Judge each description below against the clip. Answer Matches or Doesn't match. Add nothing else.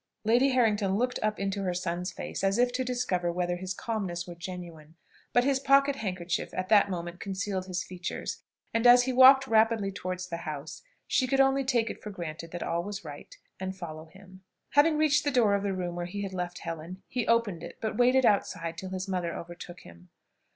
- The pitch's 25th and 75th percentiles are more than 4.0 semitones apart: Matches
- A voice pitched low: Doesn't match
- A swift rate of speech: Matches